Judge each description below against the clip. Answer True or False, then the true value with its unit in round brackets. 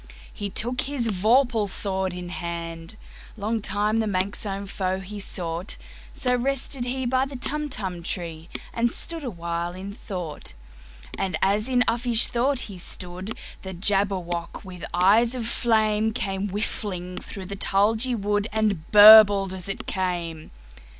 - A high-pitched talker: True (200 Hz)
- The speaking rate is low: True (125 wpm)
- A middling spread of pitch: True (3.9 semitones)